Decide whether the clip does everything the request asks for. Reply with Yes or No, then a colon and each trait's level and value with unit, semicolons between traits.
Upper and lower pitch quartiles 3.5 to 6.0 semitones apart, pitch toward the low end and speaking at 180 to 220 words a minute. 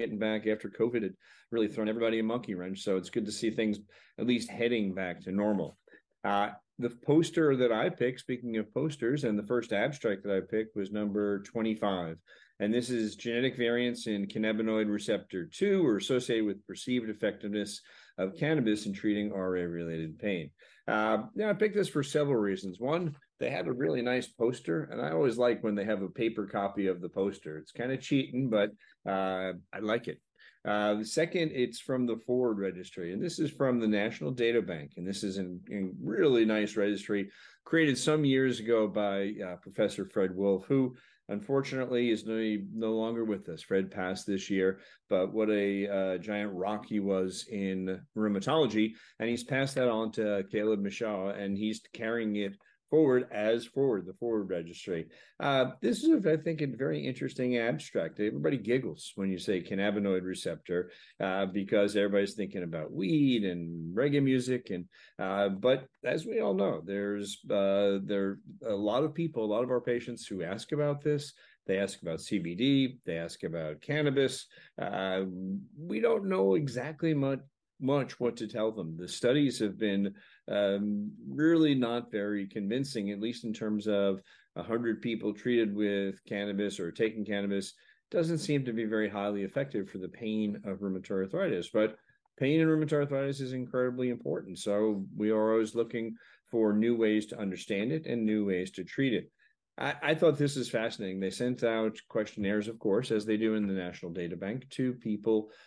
Yes: average, 3.8 semitones; low, 110 Hz; average, 185 wpm